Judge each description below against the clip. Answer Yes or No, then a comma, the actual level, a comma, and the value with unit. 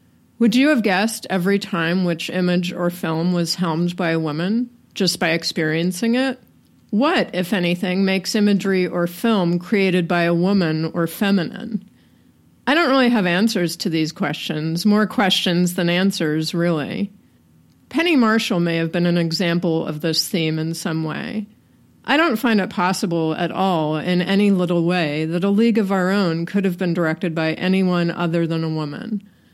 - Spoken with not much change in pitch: No, average, 3.3 semitones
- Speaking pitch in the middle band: Yes, medium, 180 Hz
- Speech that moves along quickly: No, average, 175 wpm